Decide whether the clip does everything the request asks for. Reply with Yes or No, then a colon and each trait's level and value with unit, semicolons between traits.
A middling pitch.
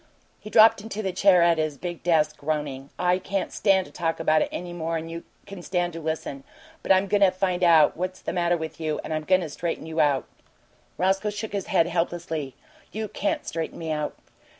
Yes: medium, 175 Hz